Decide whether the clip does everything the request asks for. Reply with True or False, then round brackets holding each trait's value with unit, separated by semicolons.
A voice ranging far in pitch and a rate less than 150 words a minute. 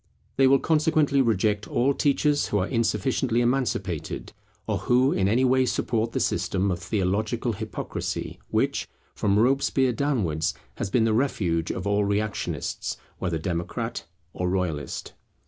True (5.7 semitones; 140 wpm)